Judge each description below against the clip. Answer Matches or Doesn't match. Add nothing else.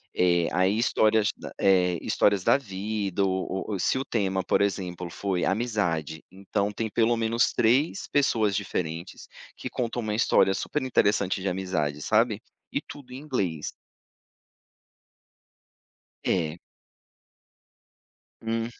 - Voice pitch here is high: Doesn't match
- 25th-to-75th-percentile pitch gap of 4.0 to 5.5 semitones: Doesn't match